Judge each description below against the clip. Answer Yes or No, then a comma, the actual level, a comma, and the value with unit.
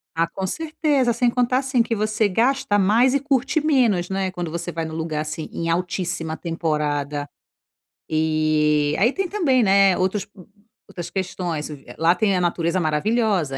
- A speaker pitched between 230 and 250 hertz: No, medium, 185 Hz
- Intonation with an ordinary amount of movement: No, wide, 6.7 semitones